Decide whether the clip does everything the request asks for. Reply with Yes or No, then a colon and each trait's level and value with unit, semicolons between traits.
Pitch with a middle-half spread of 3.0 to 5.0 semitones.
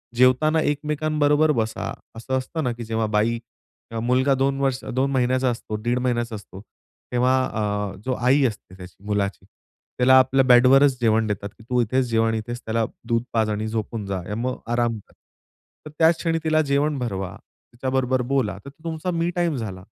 Yes: average, 3.6 semitones